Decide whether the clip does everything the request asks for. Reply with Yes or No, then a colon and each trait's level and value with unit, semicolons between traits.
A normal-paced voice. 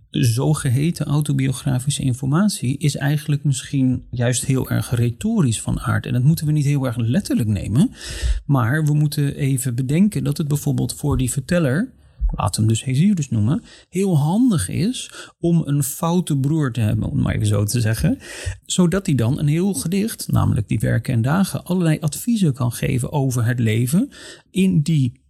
Yes: average, 175 wpm